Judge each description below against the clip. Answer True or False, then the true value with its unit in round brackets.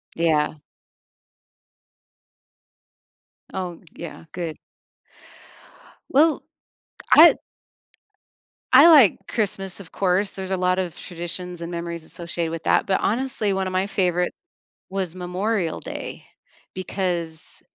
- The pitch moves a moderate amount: False (2.3 semitones)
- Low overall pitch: False (180 Hz)